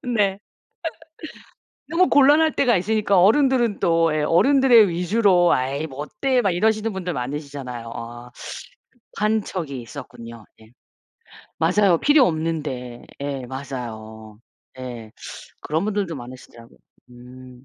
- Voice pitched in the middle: Yes, medium, 160 Hz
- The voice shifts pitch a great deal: Yes, wide, 8.9 semitones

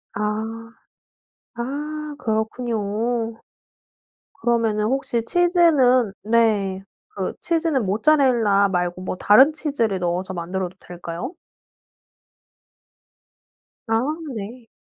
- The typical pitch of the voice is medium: No, high, 225 Hz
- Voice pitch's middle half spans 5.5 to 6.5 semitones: No, average, 5.1 semitones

